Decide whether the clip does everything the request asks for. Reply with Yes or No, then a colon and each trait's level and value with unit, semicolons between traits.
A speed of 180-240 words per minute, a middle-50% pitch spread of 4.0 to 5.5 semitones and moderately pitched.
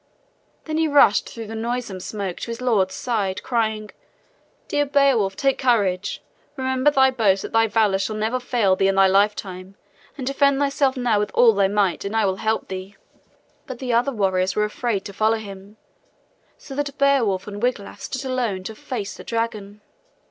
No: average, 185 wpm; average, 4.3 semitones; high, 220 Hz